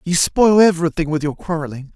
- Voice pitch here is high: No, medium, 165 Hz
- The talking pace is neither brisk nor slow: Yes, average, 185 wpm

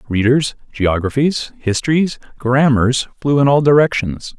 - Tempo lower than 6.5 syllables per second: Yes, 4.3 syllables/s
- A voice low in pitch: Yes, low, 130 Hz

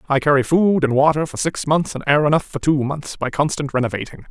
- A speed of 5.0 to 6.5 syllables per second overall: Yes, 5.9 syllables/s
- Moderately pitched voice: Yes, medium, 145 Hz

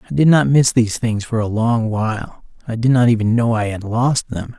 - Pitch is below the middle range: Yes, low, 115 Hz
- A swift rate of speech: Yes, fast, 250 wpm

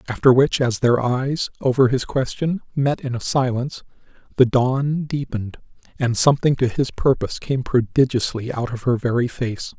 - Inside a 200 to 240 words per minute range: No, average, 165 wpm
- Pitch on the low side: Yes, low, 130 Hz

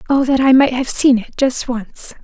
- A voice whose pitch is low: No, very high, 255 Hz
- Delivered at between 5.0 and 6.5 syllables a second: No, 4.6 syllables/s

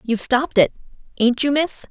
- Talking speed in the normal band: Yes, average, 155 wpm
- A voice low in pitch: No, very high, 255 Hz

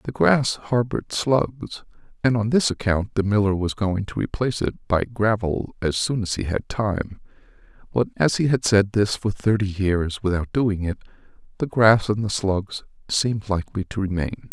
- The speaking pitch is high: No, low, 105 Hz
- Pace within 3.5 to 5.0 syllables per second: Yes, 4.7 syllables/s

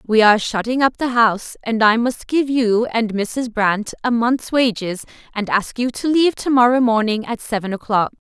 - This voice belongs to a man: No, female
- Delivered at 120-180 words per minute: No, fast, 205 wpm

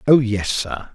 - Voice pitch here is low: Yes, low, 115 Hz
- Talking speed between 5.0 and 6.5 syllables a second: No, 3.8 syllables/s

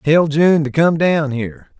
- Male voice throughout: Yes, male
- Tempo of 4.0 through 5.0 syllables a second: Yes, 4.3 syllables/s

